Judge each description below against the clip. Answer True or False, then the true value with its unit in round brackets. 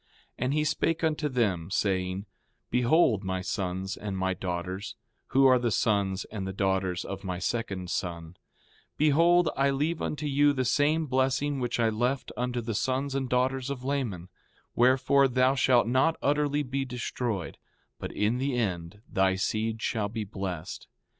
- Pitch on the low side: True (120 Hz)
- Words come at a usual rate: True (165 wpm)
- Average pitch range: False (6.1 semitones)